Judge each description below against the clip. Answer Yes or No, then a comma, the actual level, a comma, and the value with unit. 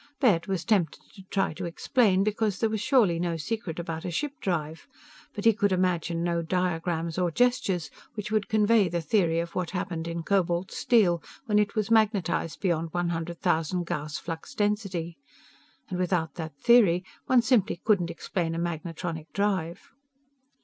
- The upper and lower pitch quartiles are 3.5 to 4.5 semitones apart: Yes, average, 3.8 semitones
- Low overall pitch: No, medium, 180 Hz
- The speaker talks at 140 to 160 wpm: No, average, 170 wpm